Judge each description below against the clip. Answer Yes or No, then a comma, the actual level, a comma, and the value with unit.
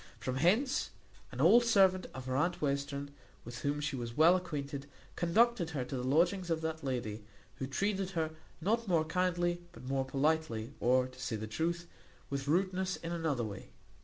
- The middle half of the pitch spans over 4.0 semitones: Yes, average, 5.2 semitones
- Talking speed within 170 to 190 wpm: Yes, average, 180 wpm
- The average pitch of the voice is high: No, medium, 160 Hz